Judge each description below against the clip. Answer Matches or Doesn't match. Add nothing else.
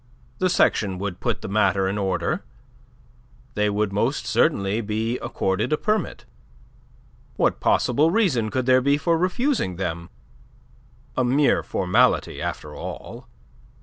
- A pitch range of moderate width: Doesn't match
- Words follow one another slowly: Matches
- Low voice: Matches